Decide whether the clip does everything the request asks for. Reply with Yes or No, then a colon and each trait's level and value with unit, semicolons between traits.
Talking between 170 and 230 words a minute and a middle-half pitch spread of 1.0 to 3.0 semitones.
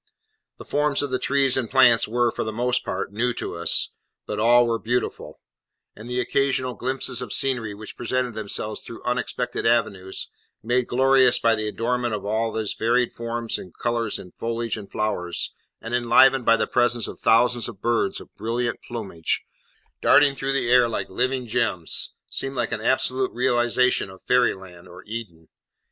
Yes: average, 175 wpm; narrow, 2.5 semitones